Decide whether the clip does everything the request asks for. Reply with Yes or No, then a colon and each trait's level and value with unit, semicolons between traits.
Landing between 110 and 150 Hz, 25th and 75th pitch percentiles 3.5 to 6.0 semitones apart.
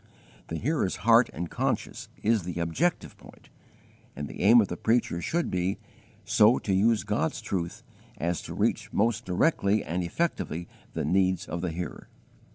No: very low, 95 Hz; average, 4.8 semitones